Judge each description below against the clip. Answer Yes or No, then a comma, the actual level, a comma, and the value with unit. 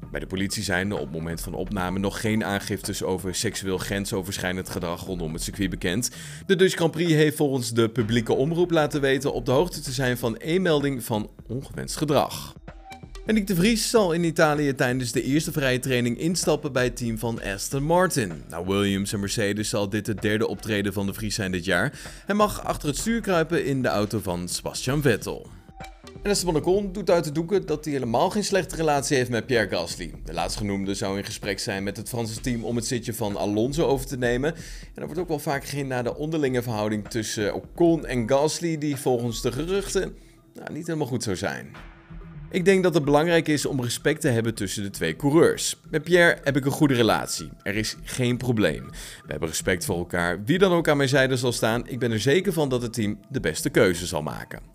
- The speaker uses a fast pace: Yes, fast, 220 wpm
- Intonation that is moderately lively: No, wide, 7.1 semitones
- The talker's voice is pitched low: Yes, low, 125 Hz